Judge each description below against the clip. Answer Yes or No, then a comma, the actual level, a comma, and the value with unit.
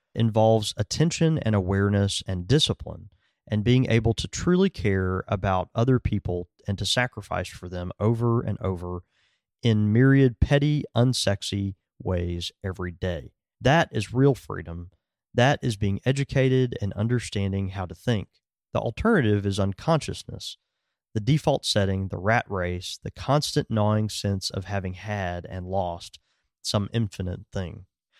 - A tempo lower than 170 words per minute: Yes, average, 140 wpm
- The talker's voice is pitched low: Yes, low, 105 Hz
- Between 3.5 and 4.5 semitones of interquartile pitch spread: Yes, average, 4.2 semitones